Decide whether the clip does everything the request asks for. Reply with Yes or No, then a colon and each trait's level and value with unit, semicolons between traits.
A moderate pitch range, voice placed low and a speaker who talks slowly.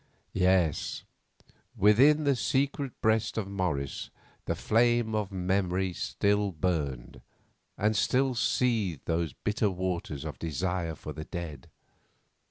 Yes: average, 4.9 semitones; very low, 95 Hz; slow, 115 wpm